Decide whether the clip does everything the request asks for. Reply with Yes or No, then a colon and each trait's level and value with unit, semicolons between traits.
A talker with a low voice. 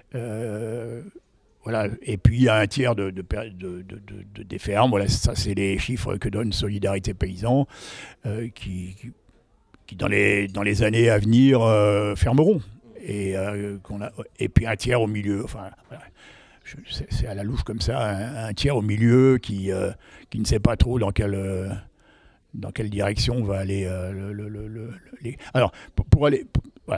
Yes: low, 105 Hz